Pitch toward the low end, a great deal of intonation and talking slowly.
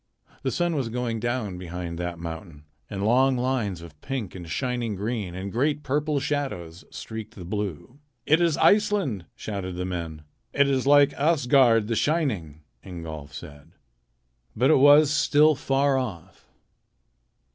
No: low, 115 Hz; wide, 7.8 semitones; average, 150 wpm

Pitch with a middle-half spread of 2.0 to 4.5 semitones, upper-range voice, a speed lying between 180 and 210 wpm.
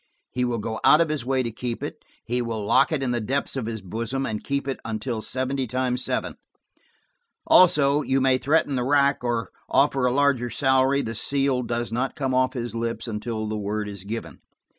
No: average, 2.9 semitones; low, 125 Hz; fast, 205 wpm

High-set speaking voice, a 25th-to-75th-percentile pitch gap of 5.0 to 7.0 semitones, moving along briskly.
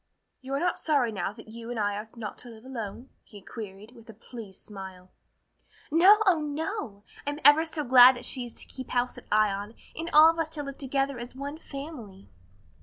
Yes: high, 245 Hz; wide, 5.4 semitones; fast, 210 wpm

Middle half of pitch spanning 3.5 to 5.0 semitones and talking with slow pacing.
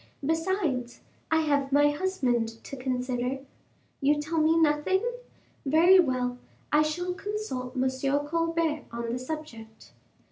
Yes: average, 4.3 semitones; slow, 120 wpm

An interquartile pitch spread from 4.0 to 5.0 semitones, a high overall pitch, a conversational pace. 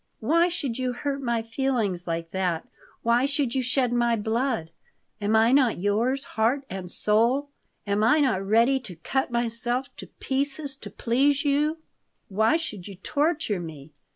Yes: average, 4.7 semitones; high, 240 Hz; average, 160 wpm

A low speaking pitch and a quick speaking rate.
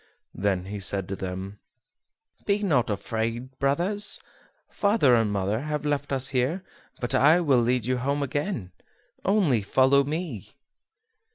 No: low, 130 Hz; average, 140 wpm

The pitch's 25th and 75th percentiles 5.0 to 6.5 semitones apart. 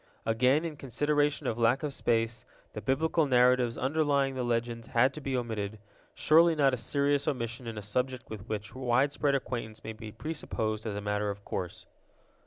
No: average, 4.1 semitones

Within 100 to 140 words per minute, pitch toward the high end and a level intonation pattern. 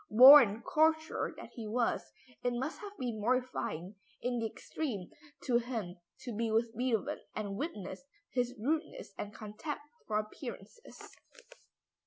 No: slow, 135 wpm; high, 235 Hz; average, 3.7 semitones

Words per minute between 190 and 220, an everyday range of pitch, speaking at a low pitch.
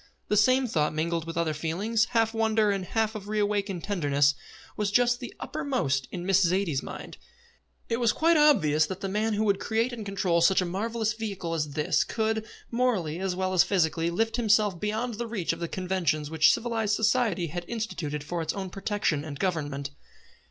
No: average, 195 wpm; average, 5.0 semitones; high, 195 Hz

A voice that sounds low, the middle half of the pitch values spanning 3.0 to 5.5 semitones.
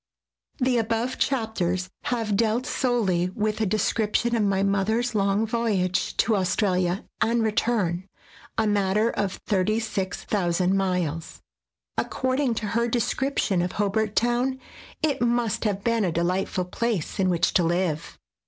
No: high, 210 Hz; average, 3.9 semitones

